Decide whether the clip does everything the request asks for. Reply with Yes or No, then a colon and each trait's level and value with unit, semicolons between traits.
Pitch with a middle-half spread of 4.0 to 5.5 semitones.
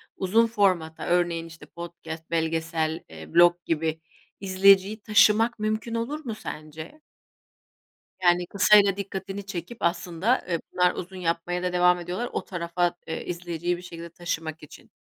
No: average, 3.1 semitones